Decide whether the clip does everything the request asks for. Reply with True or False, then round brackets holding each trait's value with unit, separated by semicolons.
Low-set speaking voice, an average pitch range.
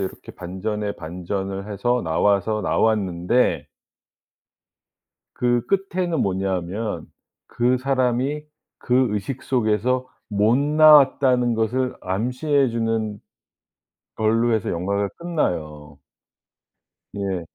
True (110 Hz; 4.7 semitones)